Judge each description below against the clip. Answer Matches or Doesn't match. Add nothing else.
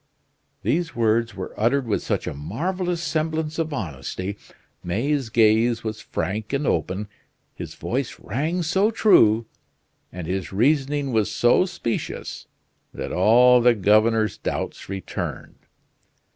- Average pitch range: Doesn't match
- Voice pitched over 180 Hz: Doesn't match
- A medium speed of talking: Doesn't match